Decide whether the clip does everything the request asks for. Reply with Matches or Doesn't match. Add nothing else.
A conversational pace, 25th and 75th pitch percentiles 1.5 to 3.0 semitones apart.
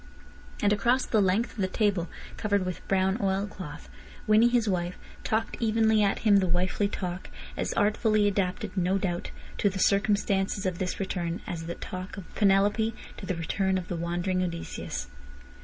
Matches